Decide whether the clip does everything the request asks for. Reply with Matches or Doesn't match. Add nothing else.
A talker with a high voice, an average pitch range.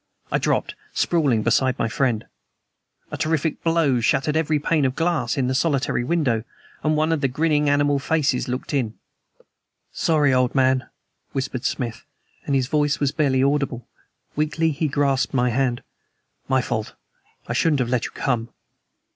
Doesn't match